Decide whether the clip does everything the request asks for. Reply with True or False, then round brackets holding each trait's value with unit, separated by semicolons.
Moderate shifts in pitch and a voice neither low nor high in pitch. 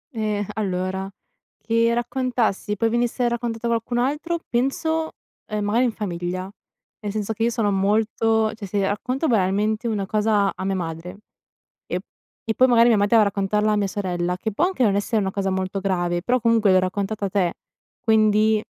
False (3.1 semitones; 210 Hz)